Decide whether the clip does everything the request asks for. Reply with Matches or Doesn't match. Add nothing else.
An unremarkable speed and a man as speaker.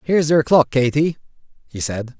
Matches